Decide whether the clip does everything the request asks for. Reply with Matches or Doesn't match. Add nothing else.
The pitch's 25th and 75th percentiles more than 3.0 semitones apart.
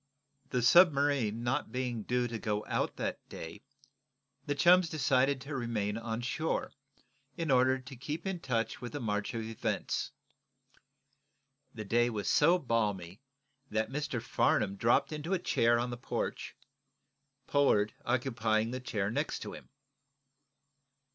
Matches